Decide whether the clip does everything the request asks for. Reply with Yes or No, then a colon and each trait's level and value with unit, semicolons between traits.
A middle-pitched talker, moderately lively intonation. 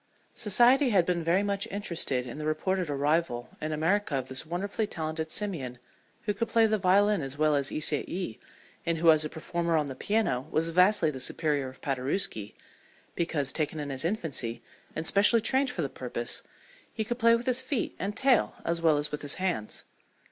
No: medium, 165 Hz; wide, 5.8 semitones